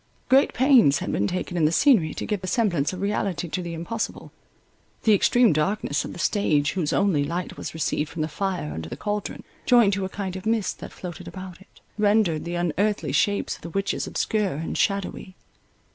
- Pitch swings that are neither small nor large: Yes, average, 4.2 semitones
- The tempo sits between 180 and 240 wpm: Yes, fast, 205 wpm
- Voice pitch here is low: No, medium, 185 Hz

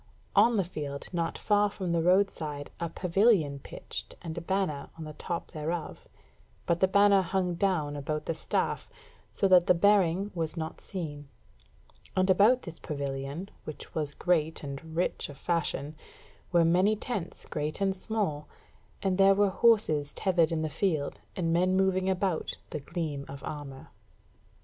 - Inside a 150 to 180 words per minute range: Yes, average, 160 wpm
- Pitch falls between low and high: Yes, medium, 170 Hz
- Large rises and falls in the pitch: No, average, 3.9 semitones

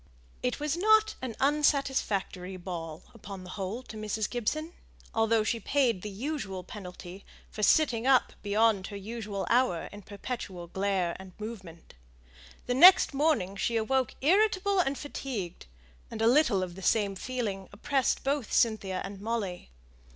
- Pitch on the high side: Yes, high, 220 Hz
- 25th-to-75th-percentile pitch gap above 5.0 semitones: Yes, wide, 5.6 semitones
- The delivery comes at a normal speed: Yes, average, 150 wpm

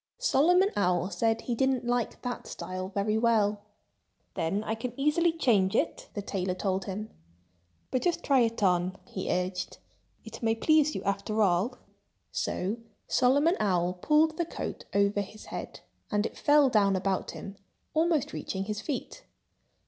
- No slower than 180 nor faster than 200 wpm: No, average, 155 wpm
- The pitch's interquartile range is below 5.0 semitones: No, wide, 5.5 semitones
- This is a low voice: No, high, 215 Hz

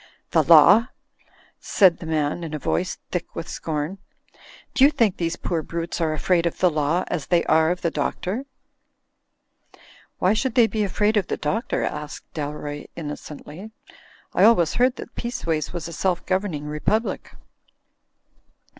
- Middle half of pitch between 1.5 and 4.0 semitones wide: No, average, 4.7 semitones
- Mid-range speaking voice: Yes, medium, 170 Hz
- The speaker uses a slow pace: No, average, 155 wpm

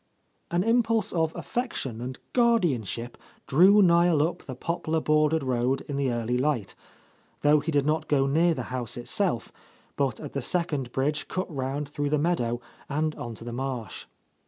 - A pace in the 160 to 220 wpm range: Yes, average, 180 wpm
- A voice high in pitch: No, medium, 145 Hz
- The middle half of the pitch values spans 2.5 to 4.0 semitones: No, average, 4.8 semitones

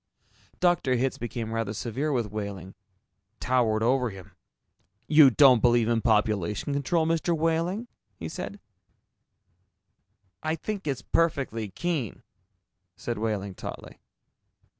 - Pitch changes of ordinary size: No, wide, 6.1 semitones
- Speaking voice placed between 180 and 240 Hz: No, low, 120 Hz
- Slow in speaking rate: Yes, slow, 115 wpm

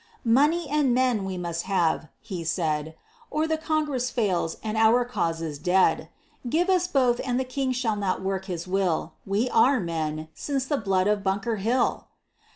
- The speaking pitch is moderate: No, high, 215 Hz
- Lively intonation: Yes, wide, 6.3 semitones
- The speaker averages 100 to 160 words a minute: No, average, 175 wpm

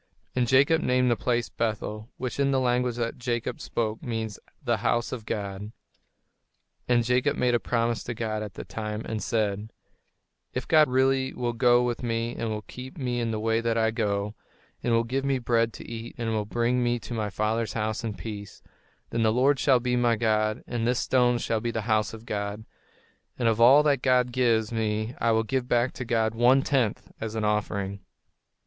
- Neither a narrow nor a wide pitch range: No, narrow, 2.2 semitones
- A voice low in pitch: Yes, low, 115 Hz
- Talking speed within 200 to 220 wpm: Yes, fast, 205 wpm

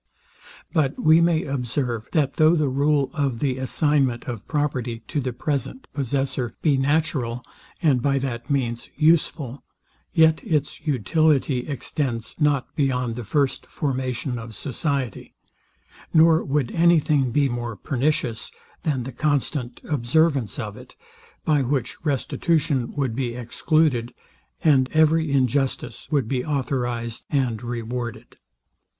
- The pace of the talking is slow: Yes, slow, 130 wpm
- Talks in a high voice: No, low, 135 Hz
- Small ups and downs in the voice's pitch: No, average, 3.5 semitones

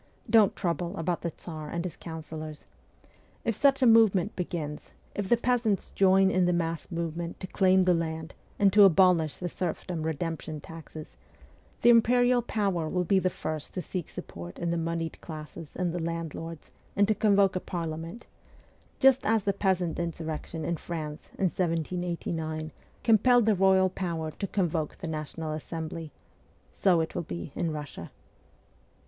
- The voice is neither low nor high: Yes, medium, 170 Hz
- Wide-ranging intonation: No, average, 3.2 semitones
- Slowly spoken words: No, average, 160 wpm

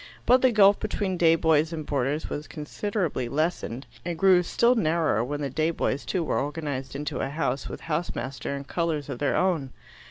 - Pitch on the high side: No, medium, 155 Hz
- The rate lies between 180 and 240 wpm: Yes, average, 195 wpm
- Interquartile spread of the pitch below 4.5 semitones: Yes, average, 4.0 semitones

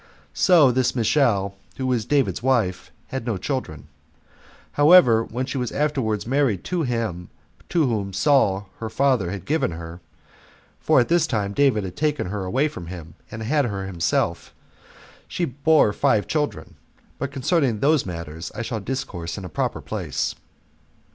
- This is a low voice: Yes, low, 115 Hz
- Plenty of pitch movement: Yes, wide, 6.4 semitones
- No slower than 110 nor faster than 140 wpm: No, average, 160 wpm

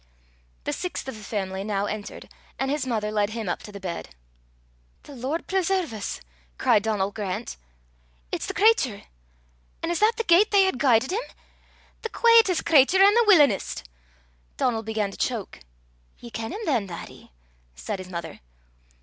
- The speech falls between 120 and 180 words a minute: Yes, average, 165 wpm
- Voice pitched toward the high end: Yes, high, 235 Hz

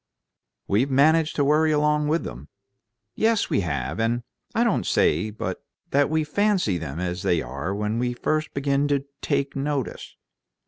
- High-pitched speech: No, medium, 140 Hz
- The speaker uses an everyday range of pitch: No, wide, 7.4 semitones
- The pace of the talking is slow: No, average, 165 wpm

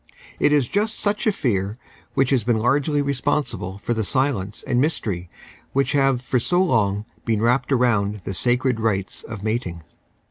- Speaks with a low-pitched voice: Yes, low, 120 Hz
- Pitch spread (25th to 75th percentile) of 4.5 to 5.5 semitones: Yes, average, 4.9 semitones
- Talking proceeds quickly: No, average, 170 wpm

